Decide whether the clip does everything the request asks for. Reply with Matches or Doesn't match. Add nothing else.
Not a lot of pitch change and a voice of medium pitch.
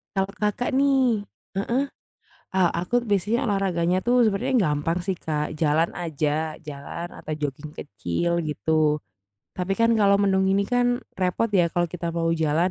Doesn't match